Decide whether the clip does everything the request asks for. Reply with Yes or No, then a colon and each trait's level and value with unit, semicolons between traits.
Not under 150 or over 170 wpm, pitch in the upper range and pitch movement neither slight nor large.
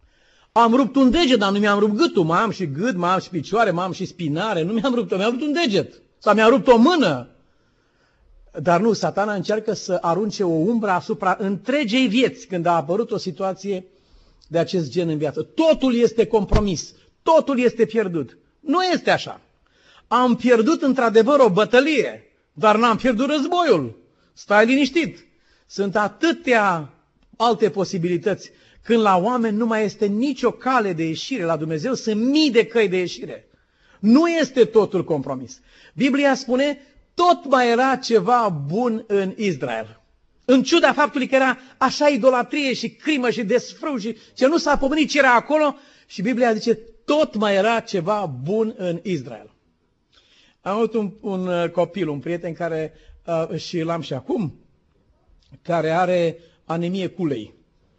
No: average, 160 wpm; high, 220 Hz; wide, 6.4 semitones